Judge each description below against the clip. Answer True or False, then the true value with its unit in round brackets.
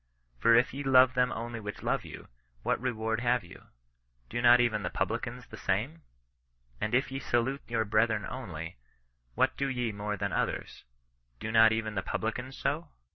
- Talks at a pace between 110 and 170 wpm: False (180 wpm)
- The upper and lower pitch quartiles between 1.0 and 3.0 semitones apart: True (2.7 semitones)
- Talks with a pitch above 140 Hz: False (115 Hz)